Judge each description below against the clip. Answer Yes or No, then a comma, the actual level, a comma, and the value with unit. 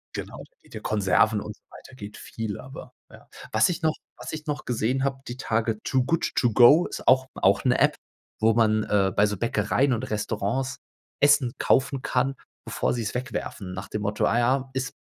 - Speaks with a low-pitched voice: Yes, low, 120 Hz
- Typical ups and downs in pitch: Yes, average, 3.7 semitones